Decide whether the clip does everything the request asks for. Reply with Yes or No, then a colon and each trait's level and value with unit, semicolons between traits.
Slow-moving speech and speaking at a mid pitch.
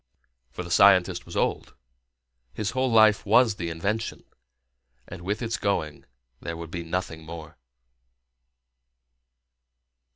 No: slow, 120 wpm; very low, 90 Hz